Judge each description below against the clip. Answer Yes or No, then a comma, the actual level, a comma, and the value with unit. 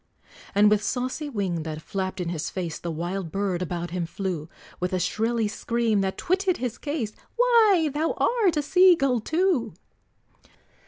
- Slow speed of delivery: No, average, 165 wpm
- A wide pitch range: Yes, wide, 8.9 semitones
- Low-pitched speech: No, high, 215 Hz